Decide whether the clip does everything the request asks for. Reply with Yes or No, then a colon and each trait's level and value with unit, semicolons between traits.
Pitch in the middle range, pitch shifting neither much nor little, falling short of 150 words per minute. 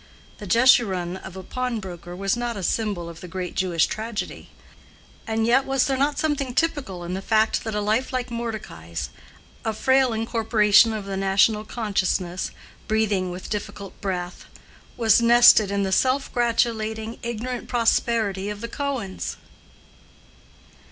No: high, 220 Hz; average, 3.7 semitones; average, 140 wpm